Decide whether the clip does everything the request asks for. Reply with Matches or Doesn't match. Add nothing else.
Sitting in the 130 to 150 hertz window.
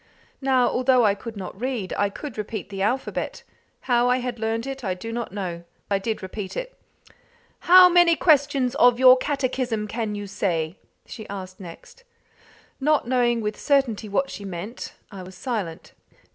Doesn't match